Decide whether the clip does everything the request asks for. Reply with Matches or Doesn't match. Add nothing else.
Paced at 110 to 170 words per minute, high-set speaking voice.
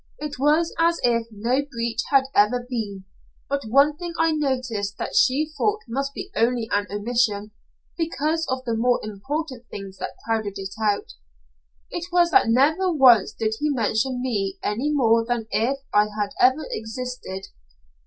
Matches